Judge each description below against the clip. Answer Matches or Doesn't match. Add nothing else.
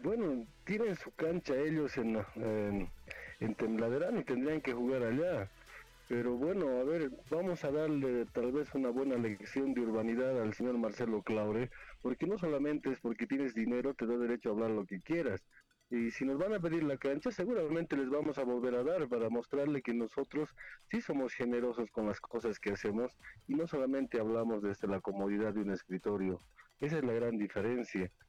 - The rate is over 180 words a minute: Matches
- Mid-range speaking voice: Doesn't match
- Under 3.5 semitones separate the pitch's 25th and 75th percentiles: Doesn't match